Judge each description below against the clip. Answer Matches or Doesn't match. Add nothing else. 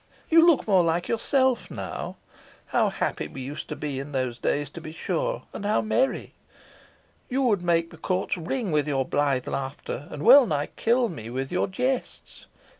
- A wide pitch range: Matches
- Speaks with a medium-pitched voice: Matches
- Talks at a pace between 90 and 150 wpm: Doesn't match